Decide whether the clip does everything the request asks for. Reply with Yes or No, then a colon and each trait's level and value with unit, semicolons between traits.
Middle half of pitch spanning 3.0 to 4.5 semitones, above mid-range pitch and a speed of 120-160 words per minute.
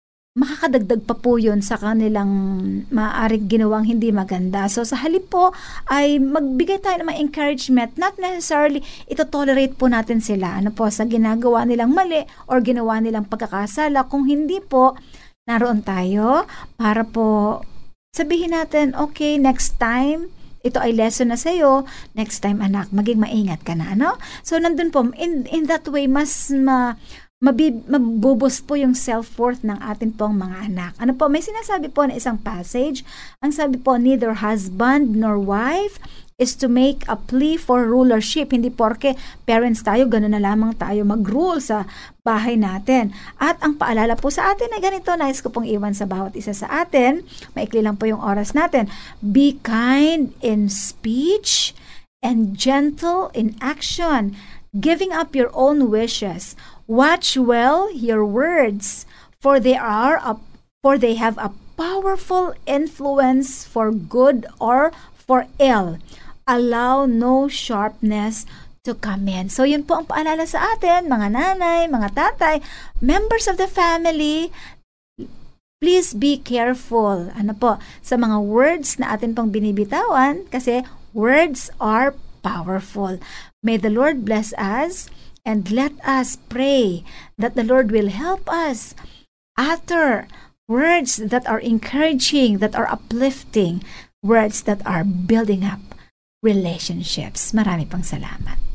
No: average, 5.1 semitones; very high, 250 Hz; average, 145 wpm